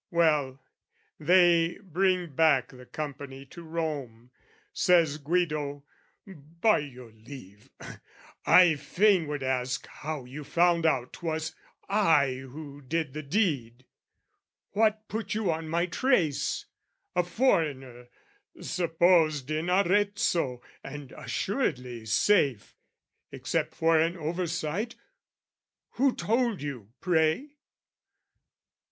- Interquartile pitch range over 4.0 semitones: Yes, average, 4.6 semitones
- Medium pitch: Yes, medium, 160 Hz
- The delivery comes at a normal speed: No, slow, 100 wpm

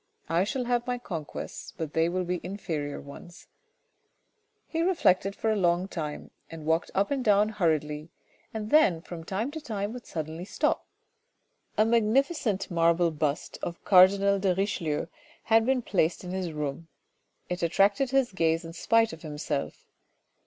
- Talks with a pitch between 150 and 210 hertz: Yes, medium, 185 Hz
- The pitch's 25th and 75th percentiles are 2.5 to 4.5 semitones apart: No, average, 5.1 semitones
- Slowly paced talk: No, average, 160 wpm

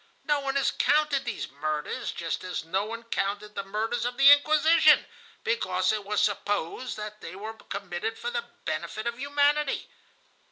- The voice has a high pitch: Yes, high, 220 Hz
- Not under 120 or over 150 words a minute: No, average, 165 wpm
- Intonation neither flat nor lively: No, wide, 6.0 semitones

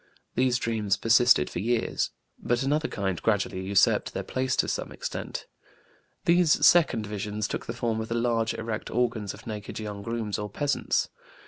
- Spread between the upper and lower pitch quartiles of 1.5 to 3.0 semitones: Yes, average, 2.7 semitones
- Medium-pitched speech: No, low, 115 Hz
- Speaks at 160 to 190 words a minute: Yes, average, 165 wpm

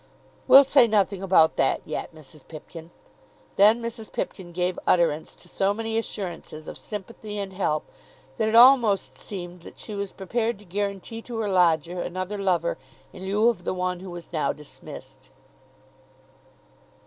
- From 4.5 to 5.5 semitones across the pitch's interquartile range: No, average, 3.6 semitones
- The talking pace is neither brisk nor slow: Yes, average, 160 wpm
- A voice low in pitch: No, high, 190 Hz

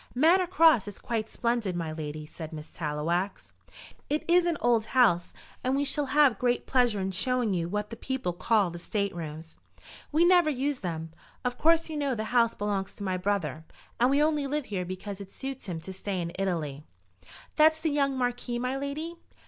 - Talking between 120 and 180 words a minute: No, average, 195 wpm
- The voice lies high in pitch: Yes, high, 230 Hz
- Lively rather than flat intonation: Yes, wide, 7.4 semitones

